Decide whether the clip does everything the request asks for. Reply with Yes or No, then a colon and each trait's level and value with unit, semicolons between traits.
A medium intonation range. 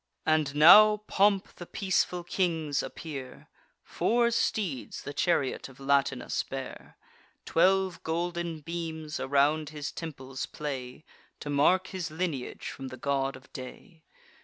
Yes: average, 4.2 semitones